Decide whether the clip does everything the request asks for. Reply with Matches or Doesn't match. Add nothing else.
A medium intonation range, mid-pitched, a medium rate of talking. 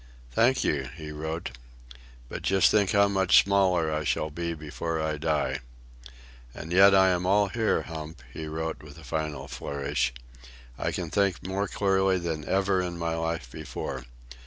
Doesn't match